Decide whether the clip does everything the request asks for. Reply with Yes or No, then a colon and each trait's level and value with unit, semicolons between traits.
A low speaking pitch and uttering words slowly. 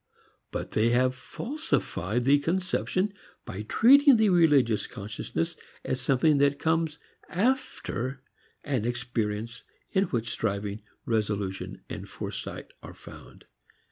Yes: low, 130 Hz; slow, 110 wpm